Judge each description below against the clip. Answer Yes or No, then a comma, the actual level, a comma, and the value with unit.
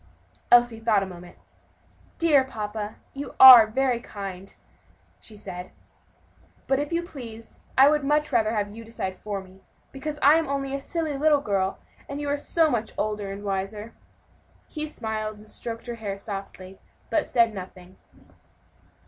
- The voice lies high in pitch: Yes, high, 225 Hz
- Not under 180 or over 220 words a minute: No, average, 160 wpm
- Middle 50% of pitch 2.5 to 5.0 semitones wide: No, wide, 5.5 semitones